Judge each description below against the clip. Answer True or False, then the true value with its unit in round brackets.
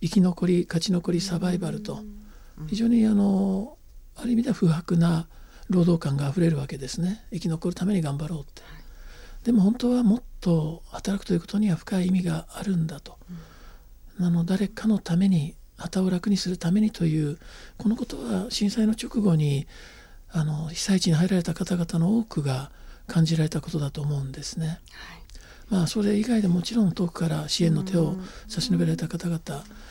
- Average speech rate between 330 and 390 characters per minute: True (345 characters per minute)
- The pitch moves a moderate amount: True (3.6 semitones)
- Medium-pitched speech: True (180 Hz)